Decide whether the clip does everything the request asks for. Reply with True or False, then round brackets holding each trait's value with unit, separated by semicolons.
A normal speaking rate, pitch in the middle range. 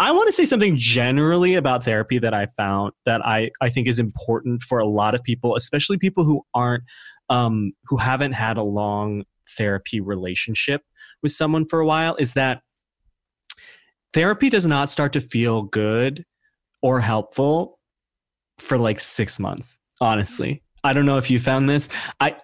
False (170 wpm; 125 Hz)